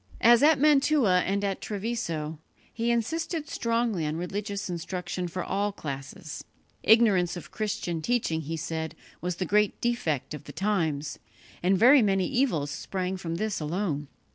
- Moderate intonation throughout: No, wide, 5.8 semitones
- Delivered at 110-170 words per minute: Yes, average, 150 wpm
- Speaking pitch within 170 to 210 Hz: Yes, high, 190 Hz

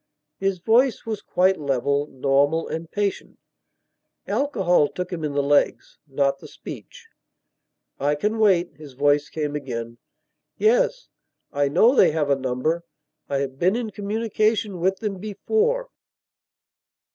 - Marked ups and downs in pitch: Yes, wide, 7.0 semitones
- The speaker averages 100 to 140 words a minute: Yes, slow, 135 wpm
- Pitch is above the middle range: No, medium, 170 Hz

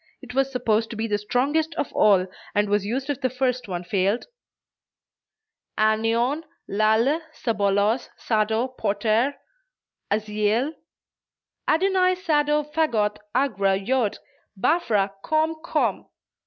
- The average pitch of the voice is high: Yes, high, 230 Hz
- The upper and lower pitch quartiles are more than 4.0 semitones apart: Yes, average, 5.2 semitones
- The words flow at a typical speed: No, slow, 115 wpm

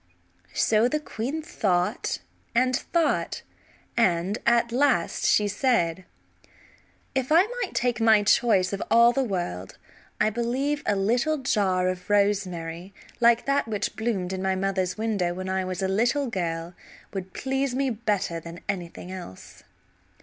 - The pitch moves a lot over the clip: No, average, 4.7 semitones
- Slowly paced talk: No, average, 145 wpm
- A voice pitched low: No, high, 205 Hz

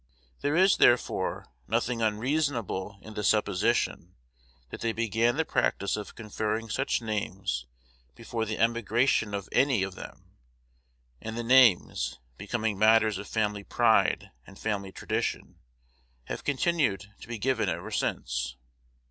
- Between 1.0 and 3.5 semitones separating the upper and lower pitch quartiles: Yes, average, 2.8 semitones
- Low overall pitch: Yes, low, 110 Hz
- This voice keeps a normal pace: No, slow, 130 wpm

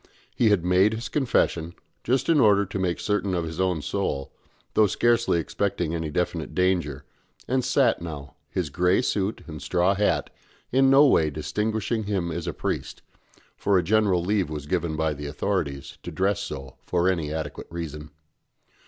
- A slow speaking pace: No, average, 170 wpm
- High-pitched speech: No, very low, 90 Hz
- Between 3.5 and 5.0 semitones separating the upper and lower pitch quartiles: Yes, average, 4.6 semitones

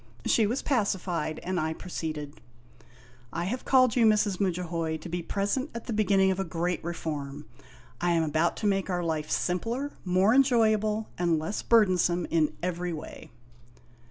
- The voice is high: No, medium, 180 Hz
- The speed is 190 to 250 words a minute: No, average, 165 wpm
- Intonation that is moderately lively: Yes, average, 4.5 semitones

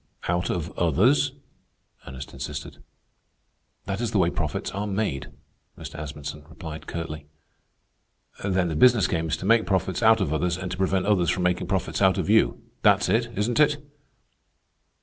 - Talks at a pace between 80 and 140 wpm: No, average, 165 wpm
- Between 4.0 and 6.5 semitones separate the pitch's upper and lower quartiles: Yes, average, 4.8 semitones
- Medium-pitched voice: No, very low, 90 Hz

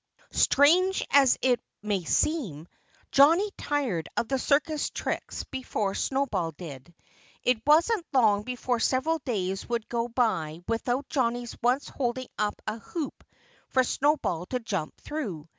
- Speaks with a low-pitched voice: No, high, 245 Hz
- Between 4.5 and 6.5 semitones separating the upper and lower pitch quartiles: Yes, wide, 5.5 semitones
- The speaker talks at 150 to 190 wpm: No, slow, 135 wpm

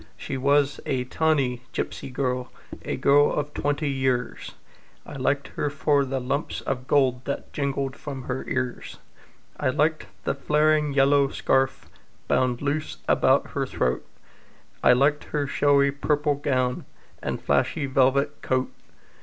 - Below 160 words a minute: Yes, average, 140 wpm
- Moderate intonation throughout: No, narrow, 2.0 semitones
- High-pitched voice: No, medium, 140 Hz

